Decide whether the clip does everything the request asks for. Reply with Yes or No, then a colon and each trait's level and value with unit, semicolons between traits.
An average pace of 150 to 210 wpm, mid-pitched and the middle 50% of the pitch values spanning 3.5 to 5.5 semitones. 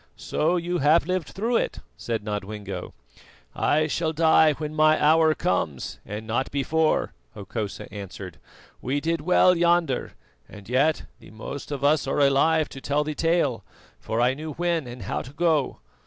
Yes: average, 165 wpm; medium, 150 Hz; average, 5.0 semitones